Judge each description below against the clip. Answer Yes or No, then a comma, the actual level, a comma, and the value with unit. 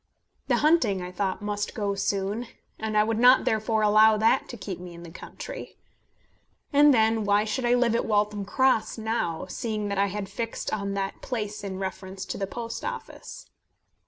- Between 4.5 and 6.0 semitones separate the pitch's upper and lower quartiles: No, narrow, 2.6 semitones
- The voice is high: Yes, high, 210 Hz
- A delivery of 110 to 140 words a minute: No, average, 190 wpm